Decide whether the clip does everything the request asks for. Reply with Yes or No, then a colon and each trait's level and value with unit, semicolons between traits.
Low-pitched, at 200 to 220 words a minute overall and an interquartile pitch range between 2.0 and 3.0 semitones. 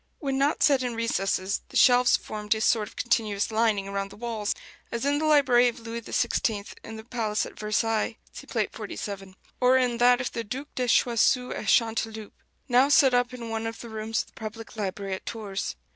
No: high, 230 Hz; fast, 205 wpm; narrow, 2.6 semitones